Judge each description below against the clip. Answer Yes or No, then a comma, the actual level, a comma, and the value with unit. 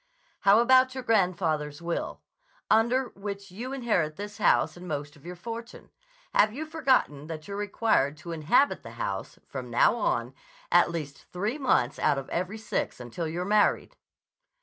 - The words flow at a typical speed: Yes, average, 165 wpm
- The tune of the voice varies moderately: No, wide, 6.8 semitones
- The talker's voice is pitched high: Yes, high, 200 Hz